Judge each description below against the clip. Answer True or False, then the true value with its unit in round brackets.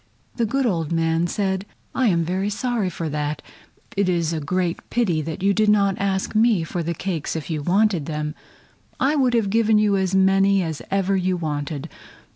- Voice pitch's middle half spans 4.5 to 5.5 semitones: False (4.0 semitones)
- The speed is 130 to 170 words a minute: False (190 wpm)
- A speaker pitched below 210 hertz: True (190 Hz)